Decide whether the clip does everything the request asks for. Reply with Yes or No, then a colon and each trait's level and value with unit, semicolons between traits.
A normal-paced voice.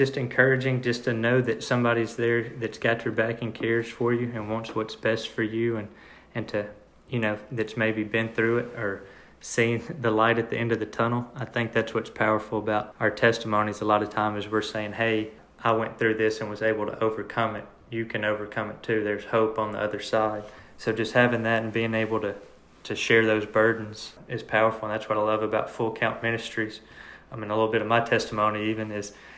No: fast, 230 wpm